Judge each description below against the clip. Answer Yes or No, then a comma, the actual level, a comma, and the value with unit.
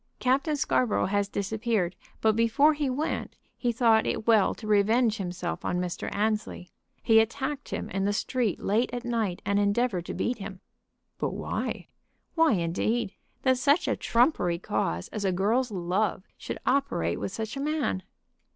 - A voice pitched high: Yes, high, 220 Hz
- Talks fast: No, average, 165 wpm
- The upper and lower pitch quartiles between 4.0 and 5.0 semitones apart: Yes, average, 4.4 semitones